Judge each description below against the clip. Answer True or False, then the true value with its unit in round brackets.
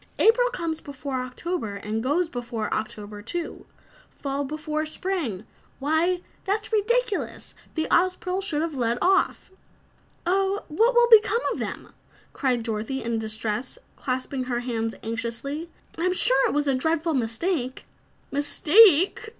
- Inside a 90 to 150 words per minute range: True (135 wpm)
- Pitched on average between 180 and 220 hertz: False (290 Hz)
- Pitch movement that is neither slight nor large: False (7.2 semitones)